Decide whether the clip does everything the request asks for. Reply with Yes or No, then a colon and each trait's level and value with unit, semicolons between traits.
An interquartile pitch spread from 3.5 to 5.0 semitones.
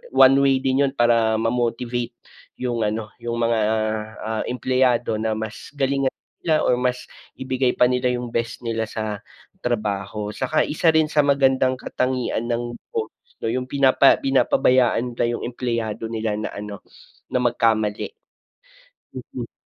No: average, 2.7 semitones